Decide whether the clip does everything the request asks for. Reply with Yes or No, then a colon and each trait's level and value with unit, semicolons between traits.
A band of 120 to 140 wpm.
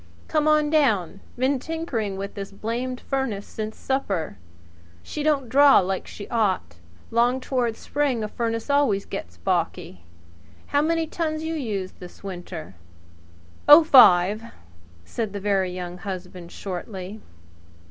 Yes: slow, 135 wpm